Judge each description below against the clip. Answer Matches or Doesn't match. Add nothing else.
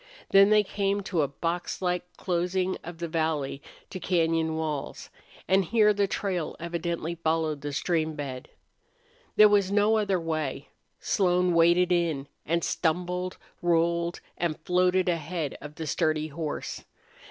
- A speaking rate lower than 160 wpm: Matches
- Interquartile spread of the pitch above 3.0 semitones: Doesn't match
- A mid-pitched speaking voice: Matches